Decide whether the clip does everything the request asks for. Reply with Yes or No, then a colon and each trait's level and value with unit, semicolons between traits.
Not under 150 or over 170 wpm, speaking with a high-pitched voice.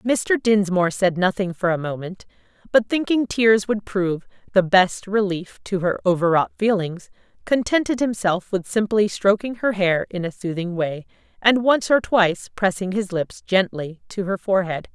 Yes: average, 165 wpm; high, 195 Hz